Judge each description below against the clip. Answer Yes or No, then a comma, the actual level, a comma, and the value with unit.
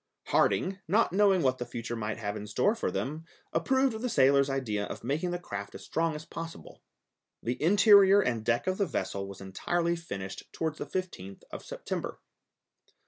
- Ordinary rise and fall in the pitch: No, wide, 8.3 semitones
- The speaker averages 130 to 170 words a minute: No, average, 180 wpm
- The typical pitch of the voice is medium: Yes, medium, 155 Hz